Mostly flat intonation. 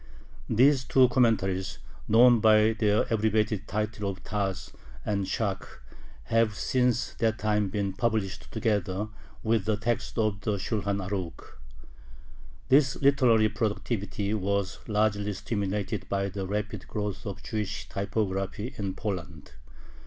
Yes: narrow, 2.1 semitones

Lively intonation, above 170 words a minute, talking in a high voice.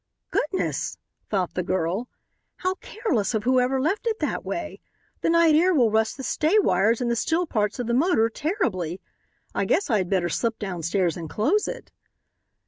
Yes: wide, 8.9 semitones; average, 180 wpm; high, 235 Hz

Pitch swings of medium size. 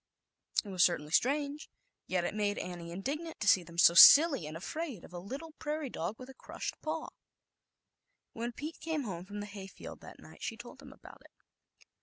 No: wide, 8.4 semitones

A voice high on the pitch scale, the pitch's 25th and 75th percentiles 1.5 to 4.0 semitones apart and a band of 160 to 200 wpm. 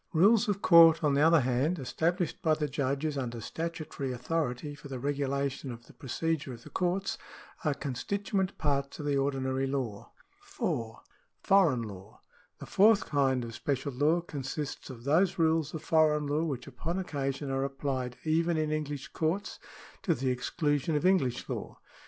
No: medium, 145 Hz; average, 3.5 semitones; average, 170 wpm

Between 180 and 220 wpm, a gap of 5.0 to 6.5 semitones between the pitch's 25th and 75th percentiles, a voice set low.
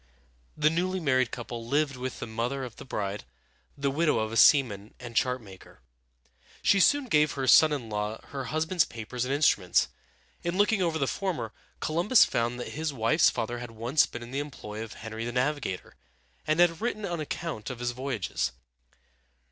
Yes: average, 185 wpm; average, 5.3 semitones; low, 130 Hz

